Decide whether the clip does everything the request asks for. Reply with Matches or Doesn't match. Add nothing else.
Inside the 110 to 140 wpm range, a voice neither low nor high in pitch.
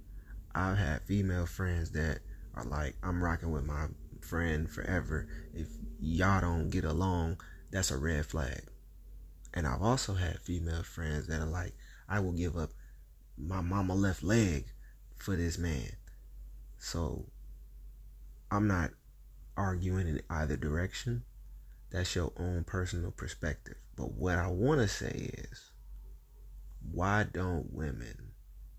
Doesn't match